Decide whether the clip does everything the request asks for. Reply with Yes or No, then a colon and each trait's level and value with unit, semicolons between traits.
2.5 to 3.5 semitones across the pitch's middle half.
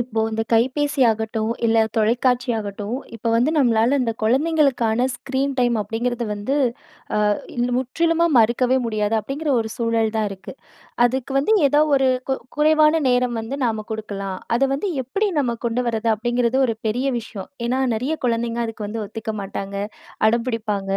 Yes: average, 3.1 semitones